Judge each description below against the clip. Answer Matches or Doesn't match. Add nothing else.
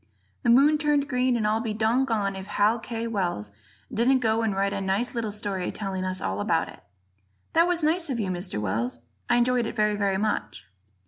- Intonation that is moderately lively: Matches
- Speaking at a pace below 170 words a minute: Doesn't match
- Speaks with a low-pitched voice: Doesn't match